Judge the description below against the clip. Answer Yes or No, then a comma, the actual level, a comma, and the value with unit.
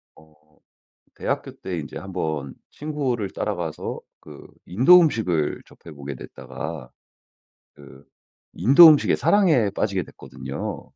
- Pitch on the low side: Yes, very low, 95 Hz